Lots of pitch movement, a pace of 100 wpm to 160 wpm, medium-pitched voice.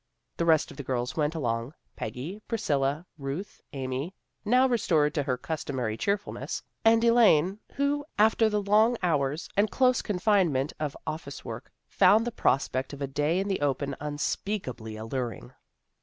Yes: wide, 7.3 semitones; average, 155 wpm; medium, 155 Hz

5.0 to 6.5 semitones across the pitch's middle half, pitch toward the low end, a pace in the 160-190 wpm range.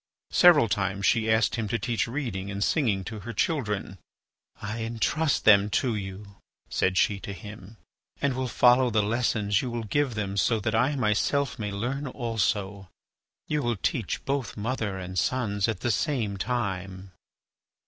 No: average, 3.7 semitones; low, 110 Hz; average, 165 wpm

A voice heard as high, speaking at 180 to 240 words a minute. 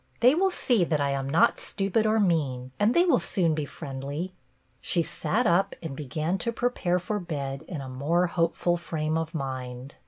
No: medium, 165 Hz; average, 195 wpm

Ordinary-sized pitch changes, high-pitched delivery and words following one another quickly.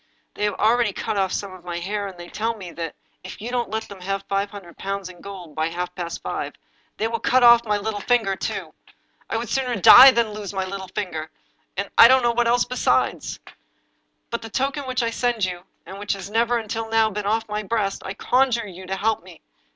Yes: average, 3.5 semitones; high, 210 Hz; fast, 240 wpm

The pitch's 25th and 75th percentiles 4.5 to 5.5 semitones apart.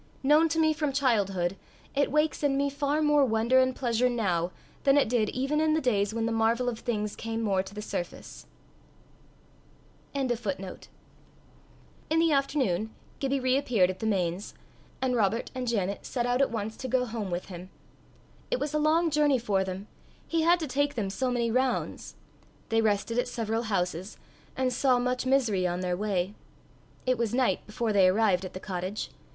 Yes: average, 5.2 semitones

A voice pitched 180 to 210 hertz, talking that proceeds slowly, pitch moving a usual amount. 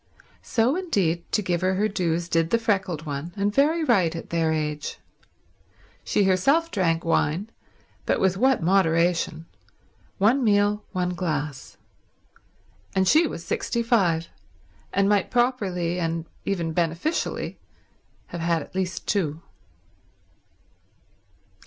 Yes: medium, 185 Hz; slow, 125 wpm; average, 4.0 semitones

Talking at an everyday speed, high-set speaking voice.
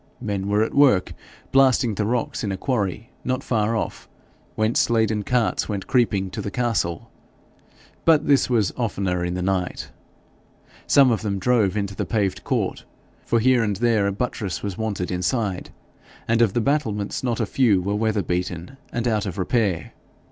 No: average, 175 wpm; low, 105 Hz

